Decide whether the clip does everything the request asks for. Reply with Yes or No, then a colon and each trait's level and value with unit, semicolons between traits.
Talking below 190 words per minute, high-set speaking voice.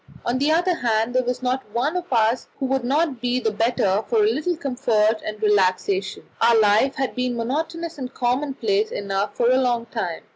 No: average, 195 wpm; very high, 250 Hz